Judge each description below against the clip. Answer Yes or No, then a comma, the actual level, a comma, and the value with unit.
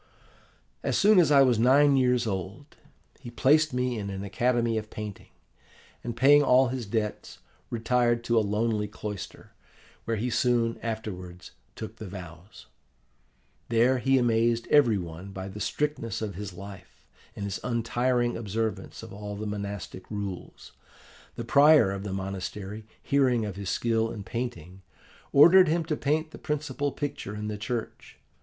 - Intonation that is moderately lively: Yes, average, 3.8 semitones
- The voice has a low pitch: Yes, low, 115 Hz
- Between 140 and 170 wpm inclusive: Yes, average, 155 wpm